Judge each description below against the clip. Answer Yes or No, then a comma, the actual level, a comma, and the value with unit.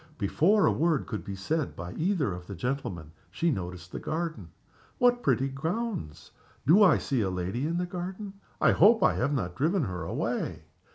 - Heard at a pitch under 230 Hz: Yes, medium, 140 Hz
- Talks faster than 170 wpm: Yes, average, 185 wpm